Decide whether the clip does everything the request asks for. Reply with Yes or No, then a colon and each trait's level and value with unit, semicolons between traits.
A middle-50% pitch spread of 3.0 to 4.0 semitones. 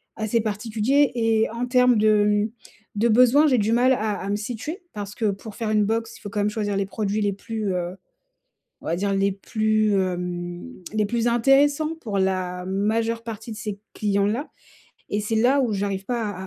No: narrow, 2.6 semitones